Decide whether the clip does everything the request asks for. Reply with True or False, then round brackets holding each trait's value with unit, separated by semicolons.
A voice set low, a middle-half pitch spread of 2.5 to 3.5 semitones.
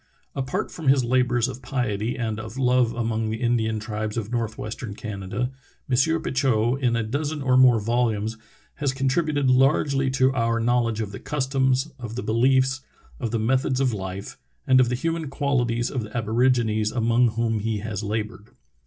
True (120 Hz; 3.0 semitones)